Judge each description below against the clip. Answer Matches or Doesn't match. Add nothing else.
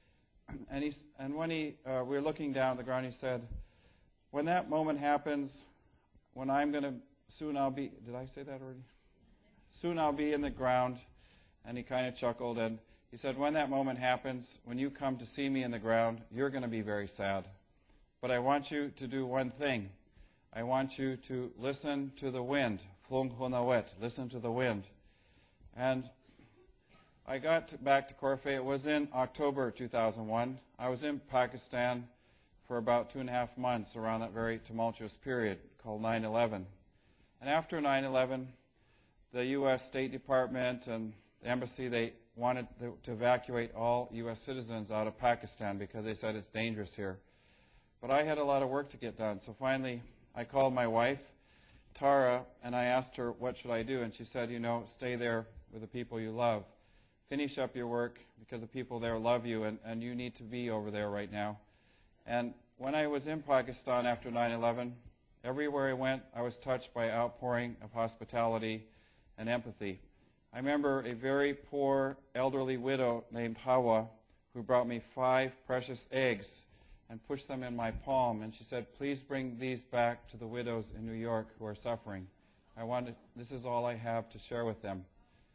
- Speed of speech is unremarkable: Matches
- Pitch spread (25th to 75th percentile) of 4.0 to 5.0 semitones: Doesn't match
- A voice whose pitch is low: Matches